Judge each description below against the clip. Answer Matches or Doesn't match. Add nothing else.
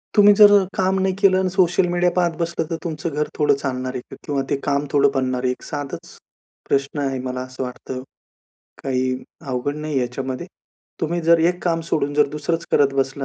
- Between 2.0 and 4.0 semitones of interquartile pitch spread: Doesn't match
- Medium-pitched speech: Matches